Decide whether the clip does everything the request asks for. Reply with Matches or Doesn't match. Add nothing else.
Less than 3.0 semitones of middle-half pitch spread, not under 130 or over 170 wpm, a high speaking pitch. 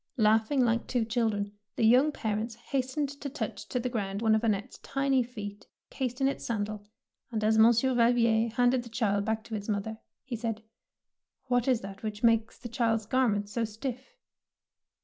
Doesn't match